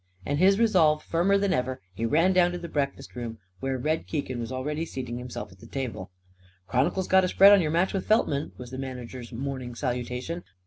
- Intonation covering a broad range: Yes, wide, 5.8 semitones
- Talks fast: Yes, fast, 210 wpm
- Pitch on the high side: No, medium, 140 Hz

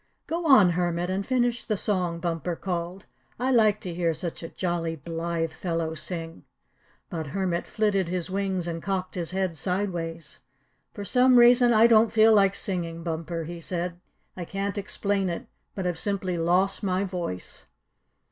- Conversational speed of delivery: Yes, average, 165 wpm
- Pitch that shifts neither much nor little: Yes, average, 3.1 semitones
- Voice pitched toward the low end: No, medium, 180 Hz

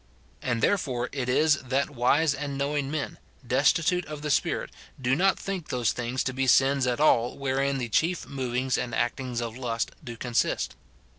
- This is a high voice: No, low, 135 Hz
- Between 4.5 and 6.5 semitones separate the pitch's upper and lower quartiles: No, average, 3.0 semitones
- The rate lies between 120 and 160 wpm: No, average, 175 wpm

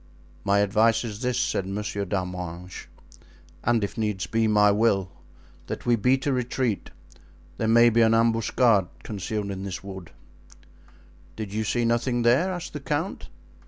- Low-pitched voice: Yes, low, 110 Hz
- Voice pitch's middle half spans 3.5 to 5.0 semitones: No, average, 3.1 semitones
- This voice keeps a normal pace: Yes, average, 155 wpm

